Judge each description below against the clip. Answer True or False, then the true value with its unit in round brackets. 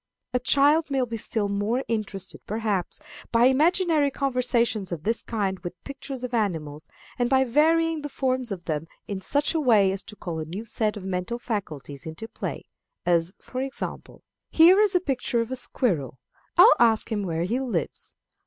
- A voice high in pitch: True (230 Hz)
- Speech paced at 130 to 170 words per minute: False (180 wpm)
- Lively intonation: True (5.8 semitones)